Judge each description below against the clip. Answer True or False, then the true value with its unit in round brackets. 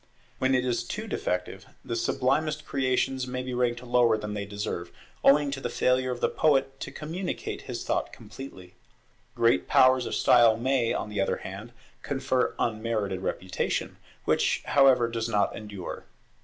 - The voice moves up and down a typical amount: True (3.5 semitones)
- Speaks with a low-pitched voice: True (125 Hz)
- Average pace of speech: True (160 wpm)